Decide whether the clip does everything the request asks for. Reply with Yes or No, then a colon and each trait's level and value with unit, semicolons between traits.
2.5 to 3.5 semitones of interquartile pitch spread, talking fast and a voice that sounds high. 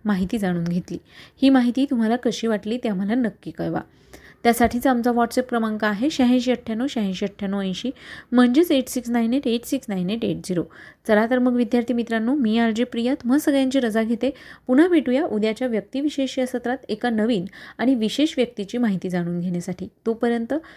Yes: average, 3.1 semitones; fast, 175 wpm; high, 240 Hz